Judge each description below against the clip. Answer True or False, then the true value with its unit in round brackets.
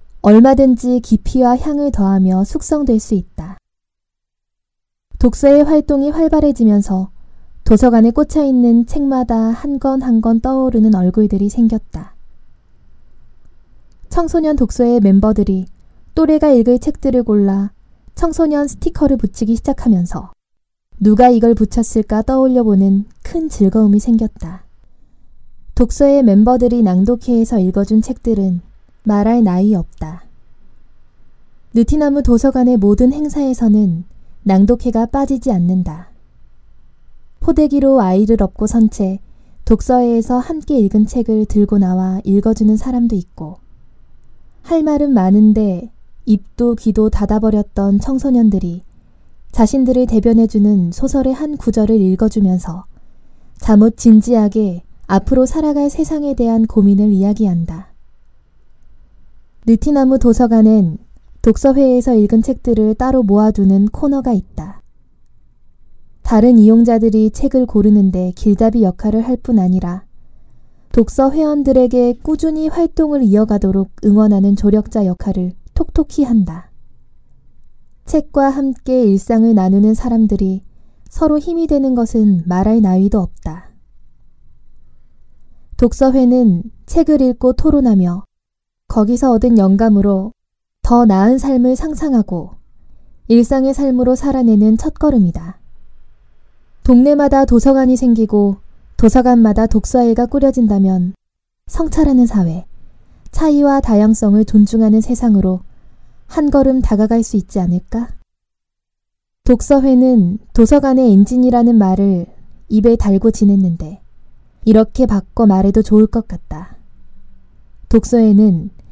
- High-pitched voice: True (225 Hz)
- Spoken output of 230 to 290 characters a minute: True (265 characters per minute)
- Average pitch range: True (4.3 semitones)